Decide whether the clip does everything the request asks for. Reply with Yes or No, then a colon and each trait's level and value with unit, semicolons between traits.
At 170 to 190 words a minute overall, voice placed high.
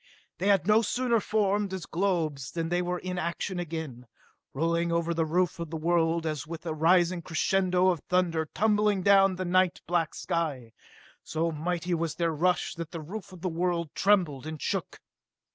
No: average, 180 wpm; medium, 170 Hz